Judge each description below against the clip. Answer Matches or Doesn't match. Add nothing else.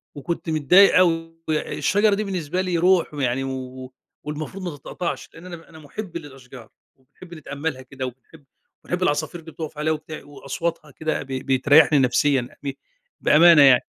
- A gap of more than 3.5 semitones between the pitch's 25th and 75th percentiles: Matches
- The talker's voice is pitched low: Doesn't match